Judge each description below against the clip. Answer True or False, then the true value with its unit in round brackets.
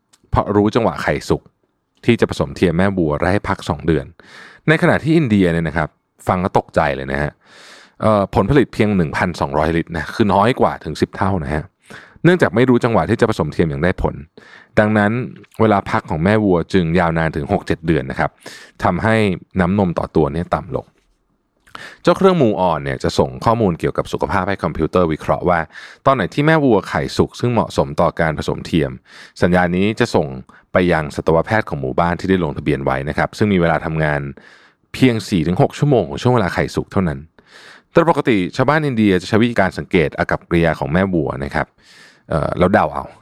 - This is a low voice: True (95 Hz)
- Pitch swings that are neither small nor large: False (5.9 semitones)